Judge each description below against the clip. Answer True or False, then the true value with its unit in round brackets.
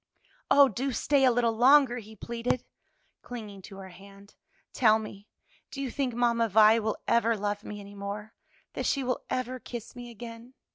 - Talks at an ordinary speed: True (180 wpm)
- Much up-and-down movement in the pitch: False (3.0 semitones)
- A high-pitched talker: True (230 Hz)